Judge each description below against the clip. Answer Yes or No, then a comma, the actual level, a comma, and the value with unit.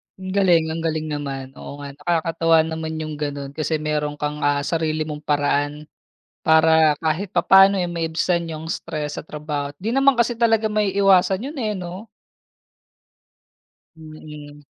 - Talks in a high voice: No, medium, 160 Hz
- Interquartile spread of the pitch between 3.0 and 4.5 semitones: Yes, average, 3.4 semitones